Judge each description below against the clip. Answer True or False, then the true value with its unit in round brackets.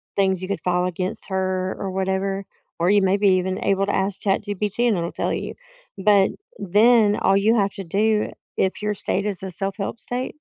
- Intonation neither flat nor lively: False (1.6 semitones)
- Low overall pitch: False (195 Hz)